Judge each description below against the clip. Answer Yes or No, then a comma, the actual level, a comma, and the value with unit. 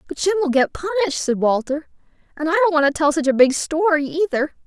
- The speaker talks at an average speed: No, fast, 230 wpm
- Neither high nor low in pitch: No, very high, 305 Hz